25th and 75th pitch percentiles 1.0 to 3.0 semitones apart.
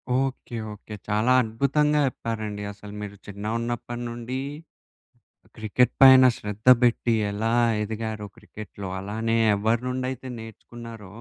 Yes: narrow, 2.5 semitones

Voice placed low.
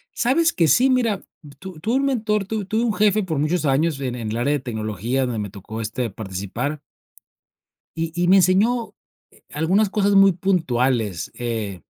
No: medium, 160 Hz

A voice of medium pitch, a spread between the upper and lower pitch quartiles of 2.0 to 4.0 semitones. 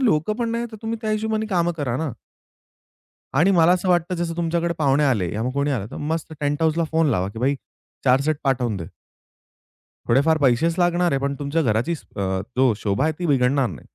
No: medium, 155 Hz; average, 4.7 semitones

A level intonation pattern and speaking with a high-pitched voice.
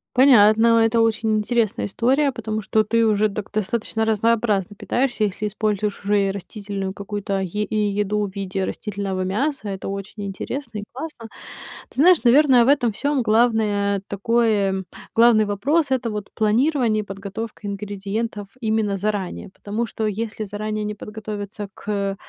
Yes: narrow, 2.3 semitones; high, 215 Hz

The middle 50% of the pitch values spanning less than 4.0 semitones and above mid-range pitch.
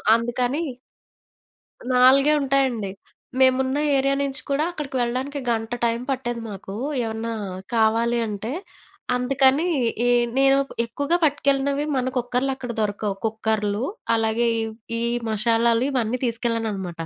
Yes: average, 3.3 semitones; high, 240 Hz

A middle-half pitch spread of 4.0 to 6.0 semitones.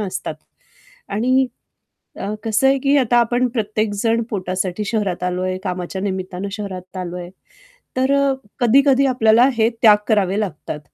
Yes: average, 4.5 semitones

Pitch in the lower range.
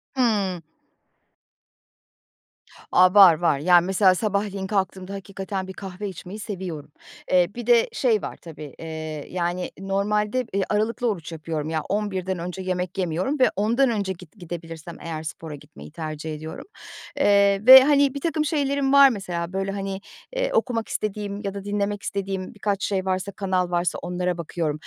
No: high, 190 Hz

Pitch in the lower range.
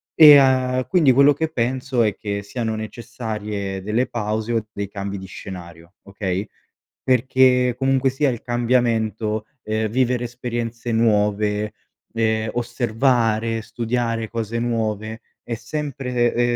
Yes: low, 115 Hz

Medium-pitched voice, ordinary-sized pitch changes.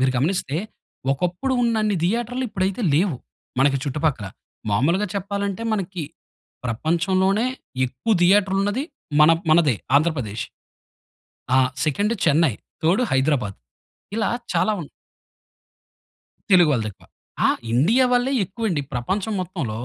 No: medium, 175 Hz; wide, 6.6 semitones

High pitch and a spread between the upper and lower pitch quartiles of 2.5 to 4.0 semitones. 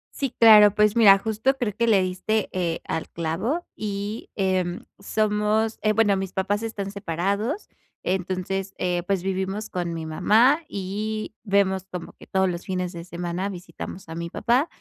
Yes: high, 195 Hz; average, 2.9 semitones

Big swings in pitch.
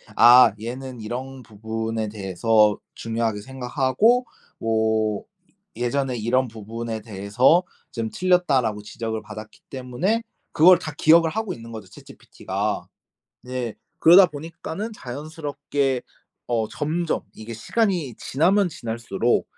Yes: wide, 5.7 semitones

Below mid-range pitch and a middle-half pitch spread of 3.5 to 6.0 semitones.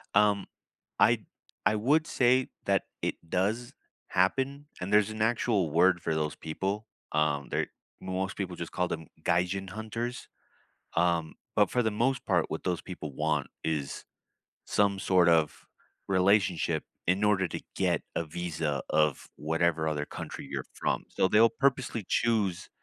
Yes: very low, 95 Hz; average, 4.8 semitones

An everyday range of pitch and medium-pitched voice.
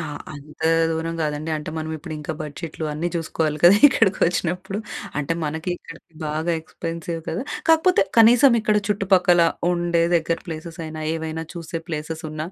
No: narrow, 2.0 semitones; medium, 165 Hz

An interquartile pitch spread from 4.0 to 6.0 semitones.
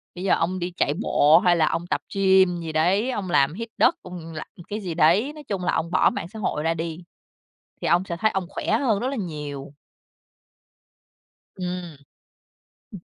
No: average, 3.2 semitones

